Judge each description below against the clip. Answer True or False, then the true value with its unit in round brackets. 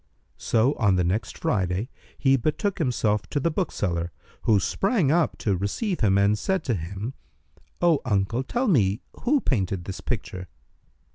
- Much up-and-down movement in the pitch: True (8.0 semitones)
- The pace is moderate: True (155 wpm)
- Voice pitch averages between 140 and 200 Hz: False (110 Hz)